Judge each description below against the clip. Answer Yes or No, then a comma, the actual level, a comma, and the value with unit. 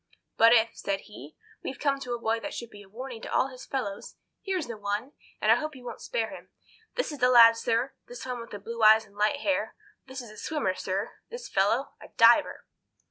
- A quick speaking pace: Yes, fast, 220 wpm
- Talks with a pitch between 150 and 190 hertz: No, high, 235 Hz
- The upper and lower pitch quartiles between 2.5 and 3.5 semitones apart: No, average, 4.0 semitones